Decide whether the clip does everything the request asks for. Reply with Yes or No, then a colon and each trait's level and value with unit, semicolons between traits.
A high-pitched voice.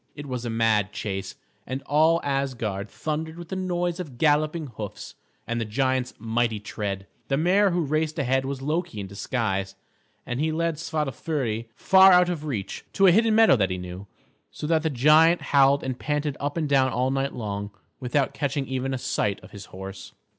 No: low, 135 Hz